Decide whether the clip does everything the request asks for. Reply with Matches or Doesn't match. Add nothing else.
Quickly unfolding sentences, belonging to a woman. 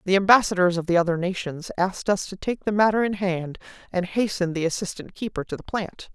Matches